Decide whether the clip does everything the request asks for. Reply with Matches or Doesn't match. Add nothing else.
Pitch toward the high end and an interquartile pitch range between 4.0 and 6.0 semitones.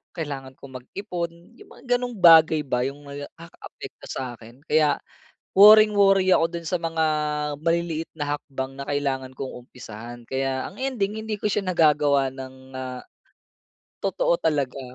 Doesn't match